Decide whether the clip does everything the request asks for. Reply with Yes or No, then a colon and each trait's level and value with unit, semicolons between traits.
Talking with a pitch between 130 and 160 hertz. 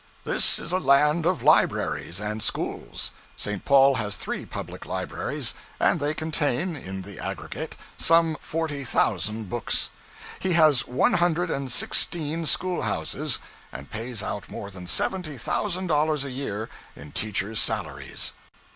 Yes: medium, 140 Hz